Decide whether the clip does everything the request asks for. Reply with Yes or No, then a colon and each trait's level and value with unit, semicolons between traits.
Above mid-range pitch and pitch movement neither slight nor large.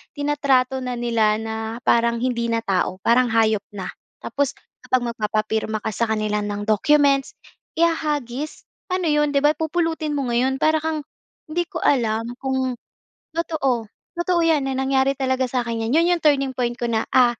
Yes: very high, 260 Hz; average, 4.4 semitones